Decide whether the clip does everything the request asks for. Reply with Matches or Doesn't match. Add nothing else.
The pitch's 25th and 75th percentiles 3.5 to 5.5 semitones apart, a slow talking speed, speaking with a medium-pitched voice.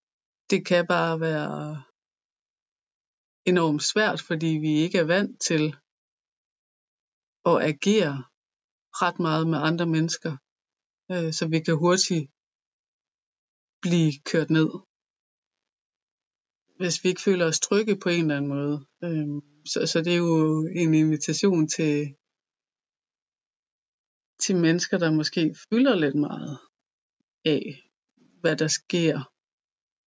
Doesn't match